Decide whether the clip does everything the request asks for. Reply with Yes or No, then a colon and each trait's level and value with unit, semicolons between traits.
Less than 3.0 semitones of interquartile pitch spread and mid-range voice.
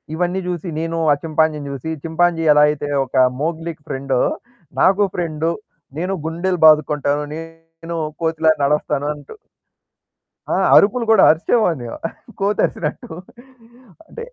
Yes: narrow, 2.6 semitones; medium, 165 Hz